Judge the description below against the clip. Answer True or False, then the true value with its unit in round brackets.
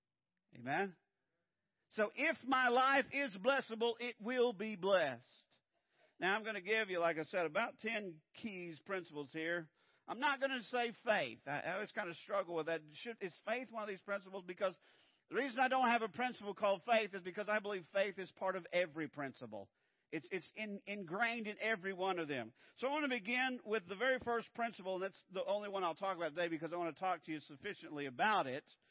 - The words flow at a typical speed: False (215 wpm)